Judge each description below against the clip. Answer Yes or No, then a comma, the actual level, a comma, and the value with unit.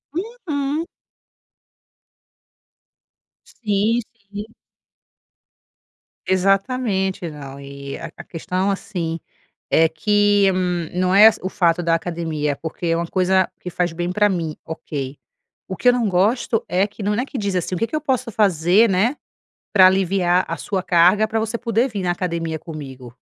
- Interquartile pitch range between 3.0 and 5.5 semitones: Yes, average, 4.1 semitones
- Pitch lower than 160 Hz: No, medium, 185 Hz